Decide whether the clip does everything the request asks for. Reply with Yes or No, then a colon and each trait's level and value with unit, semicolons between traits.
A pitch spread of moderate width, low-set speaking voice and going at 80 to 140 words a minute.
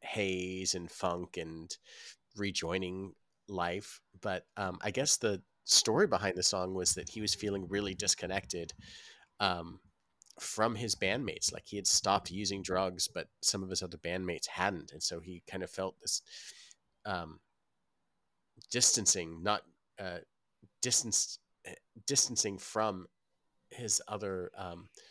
No: narrow, 2.1 semitones; very low, 95 Hz; slow, 135 wpm